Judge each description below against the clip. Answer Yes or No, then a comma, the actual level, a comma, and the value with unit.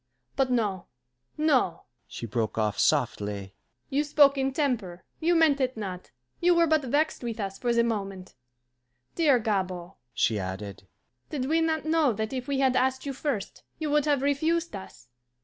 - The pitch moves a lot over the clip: Yes, wide, 7.7 semitones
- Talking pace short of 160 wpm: No, average, 170 wpm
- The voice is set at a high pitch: Yes, very high, 255 Hz